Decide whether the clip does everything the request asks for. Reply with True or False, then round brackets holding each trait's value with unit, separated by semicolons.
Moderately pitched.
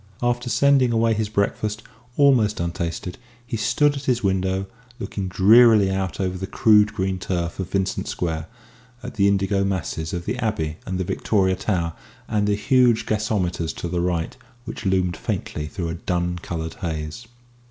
False (95 Hz)